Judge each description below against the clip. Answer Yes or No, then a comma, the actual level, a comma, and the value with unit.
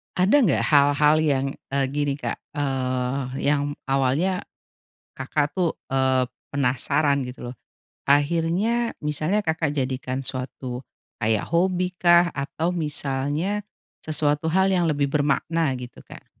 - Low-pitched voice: No, medium, 145 Hz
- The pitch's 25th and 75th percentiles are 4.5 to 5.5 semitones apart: No, average, 3.9 semitones